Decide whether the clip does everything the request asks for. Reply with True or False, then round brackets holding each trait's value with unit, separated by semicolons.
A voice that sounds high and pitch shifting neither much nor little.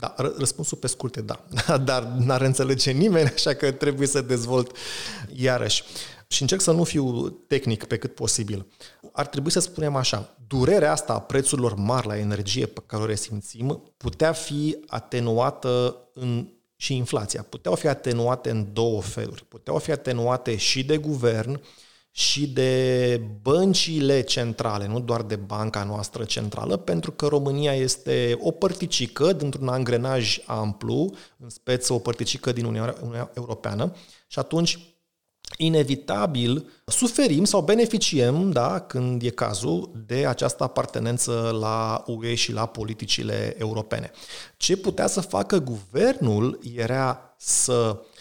False (125 Hz; 3.9 semitones)